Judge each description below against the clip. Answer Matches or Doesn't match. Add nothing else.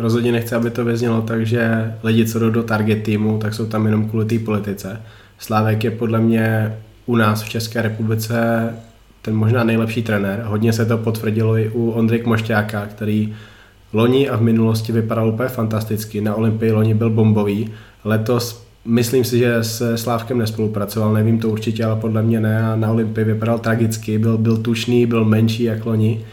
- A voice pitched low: Matches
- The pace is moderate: Doesn't match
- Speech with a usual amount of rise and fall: Doesn't match